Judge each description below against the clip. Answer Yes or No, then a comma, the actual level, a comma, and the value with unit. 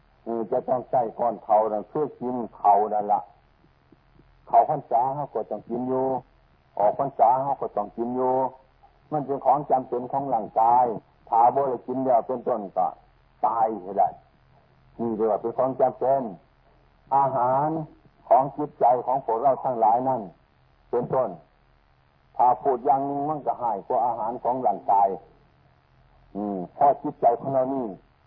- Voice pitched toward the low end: Yes, low, 120 Hz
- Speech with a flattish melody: No, average, 4.4 semitones